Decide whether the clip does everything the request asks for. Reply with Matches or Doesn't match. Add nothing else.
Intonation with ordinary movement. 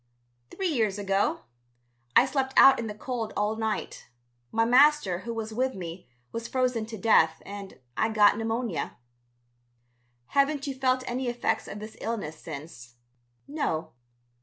Matches